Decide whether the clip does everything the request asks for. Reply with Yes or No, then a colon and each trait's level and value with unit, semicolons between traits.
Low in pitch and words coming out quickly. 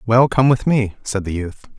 Yes: low, 115 Hz; fast, 235 wpm